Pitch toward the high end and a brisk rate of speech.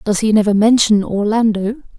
No: high, 215 Hz; average, 150 wpm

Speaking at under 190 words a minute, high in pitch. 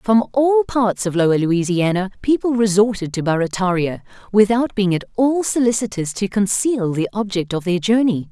Yes: average, 160 wpm; high, 205 Hz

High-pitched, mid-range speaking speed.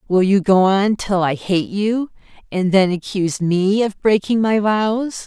Yes: high, 200 Hz; average, 180 wpm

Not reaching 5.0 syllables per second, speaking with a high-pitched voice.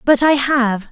Yes: 3.8 syllables/s; very high, 260 Hz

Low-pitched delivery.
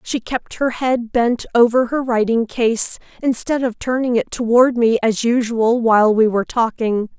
No: high, 235 Hz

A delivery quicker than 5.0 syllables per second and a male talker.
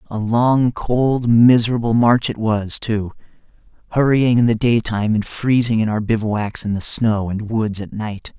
No: 4.3 syllables/s; male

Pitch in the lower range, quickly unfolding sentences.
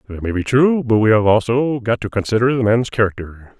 Yes: low, 115 Hz; fast, 235 wpm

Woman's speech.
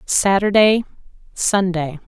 Yes: female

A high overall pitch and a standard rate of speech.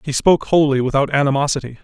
No: medium, 140 Hz; average, 165 wpm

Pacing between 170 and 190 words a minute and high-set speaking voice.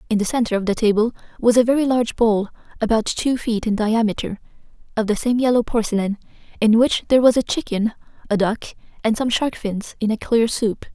No: fast, 205 wpm; high, 225 Hz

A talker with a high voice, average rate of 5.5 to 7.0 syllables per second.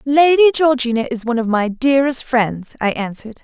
Yes: very high, 250 Hz; 5.6 syllables/s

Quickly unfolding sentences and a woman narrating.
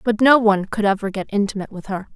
Yes: fast, 250 wpm; female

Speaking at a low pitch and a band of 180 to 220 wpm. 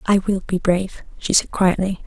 No: high, 190 Hz; fast, 205 wpm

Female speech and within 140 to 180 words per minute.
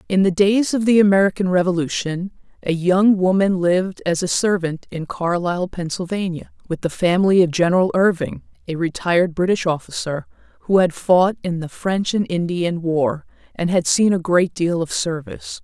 Yes: female; average, 170 wpm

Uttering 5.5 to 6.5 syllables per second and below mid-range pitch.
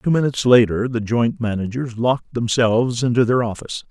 Yes: 5.7 syllables/s; low, 120 Hz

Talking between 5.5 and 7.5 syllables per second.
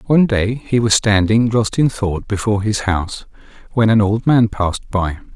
No: 5.0 syllables/s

